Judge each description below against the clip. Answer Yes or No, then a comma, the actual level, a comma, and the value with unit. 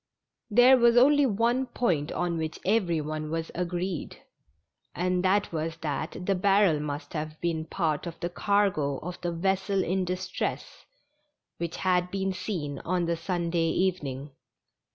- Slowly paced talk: No, average, 150 wpm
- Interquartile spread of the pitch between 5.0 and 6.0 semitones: No, average, 3.2 semitones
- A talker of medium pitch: Yes, medium, 180 Hz